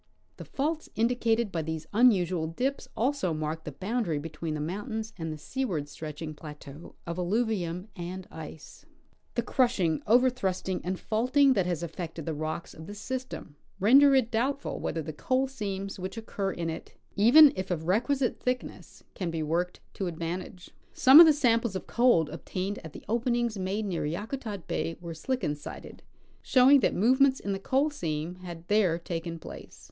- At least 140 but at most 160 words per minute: No, average, 170 wpm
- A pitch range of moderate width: No, wide, 6.7 semitones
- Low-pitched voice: No, high, 190 Hz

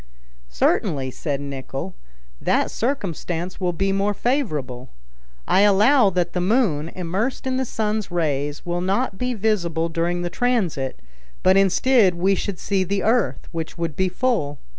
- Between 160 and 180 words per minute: No, average, 150 wpm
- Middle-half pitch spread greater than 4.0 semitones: Yes, average, 4.7 semitones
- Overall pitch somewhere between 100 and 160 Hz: No, medium, 185 Hz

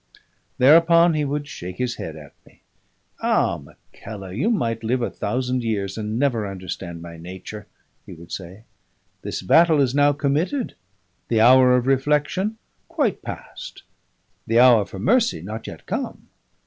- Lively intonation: Yes, wide, 6.7 semitones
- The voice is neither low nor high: No, low, 120 Hz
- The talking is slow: No, average, 150 wpm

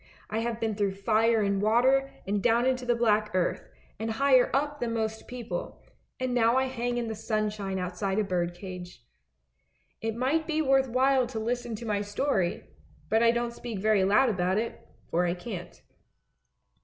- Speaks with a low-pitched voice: No, high, 225 Hz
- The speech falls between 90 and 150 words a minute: No, average, 180 wpm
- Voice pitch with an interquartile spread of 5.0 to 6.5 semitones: No, average, 3.3 semitones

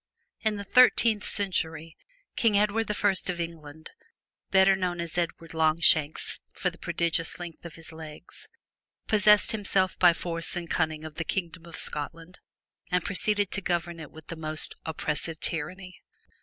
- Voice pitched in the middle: Yes, medium, 170 Hz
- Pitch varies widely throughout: No, average, 3.4 semitones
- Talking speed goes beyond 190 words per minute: No, average, 155 wpm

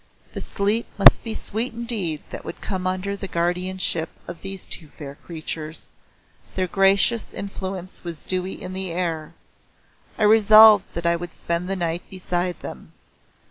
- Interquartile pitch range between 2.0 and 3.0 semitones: Yes, average, 2.7 semitones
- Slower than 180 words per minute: Yes, average, 155 wpm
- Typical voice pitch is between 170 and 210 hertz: Yes, medium, 185 Hz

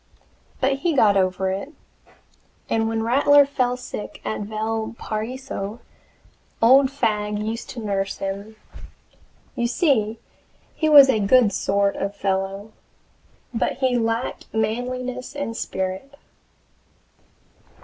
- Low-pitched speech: No, high, 225 Hz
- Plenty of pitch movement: No, average, 4.0 semitones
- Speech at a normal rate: No, slow, 110 wpm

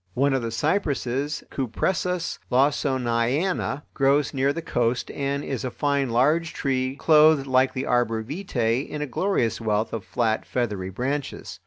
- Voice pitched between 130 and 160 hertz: Yes, low, 135 Hz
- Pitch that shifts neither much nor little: Yes, average, 3.6 semitones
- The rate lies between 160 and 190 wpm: No, average, 150 wpm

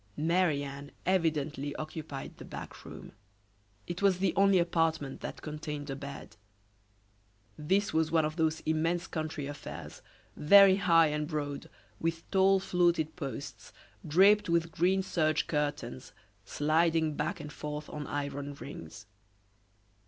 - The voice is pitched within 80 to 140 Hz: No, medium, 155 Hz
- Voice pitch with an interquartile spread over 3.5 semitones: No, average, 3.0 semitones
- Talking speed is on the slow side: Yes, slow, 130 wpm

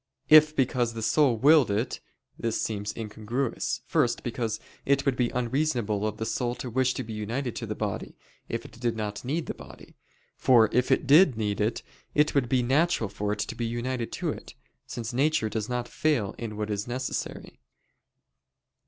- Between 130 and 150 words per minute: No, average, 190 wpm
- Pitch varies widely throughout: No, average, 3.2 semitones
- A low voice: Yes, low, 120 Hz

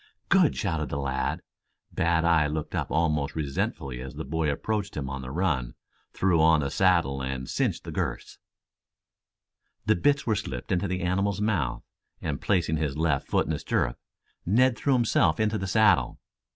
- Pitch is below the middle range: Yes, very low, 80 Hz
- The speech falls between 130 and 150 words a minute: No, average, 175 wpm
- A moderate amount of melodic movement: No, wide, 6.0 semitones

